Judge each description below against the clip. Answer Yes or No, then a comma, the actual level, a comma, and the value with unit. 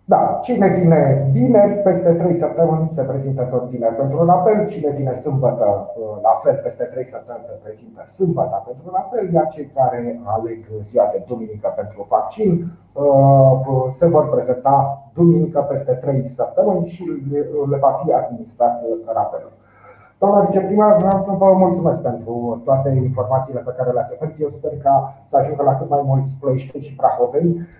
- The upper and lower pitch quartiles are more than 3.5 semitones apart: Yes, average, 5.0 semitones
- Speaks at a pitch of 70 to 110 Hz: No, medium, 140 Hz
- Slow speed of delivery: No, average, 160 wpm